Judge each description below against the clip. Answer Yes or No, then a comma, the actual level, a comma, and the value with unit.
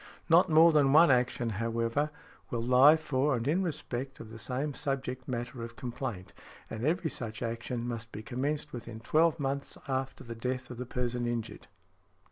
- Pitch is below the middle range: Yes, low, 125 Hz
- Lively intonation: No, average, 3.6 semitones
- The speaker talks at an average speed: Yes, average, 175 wpm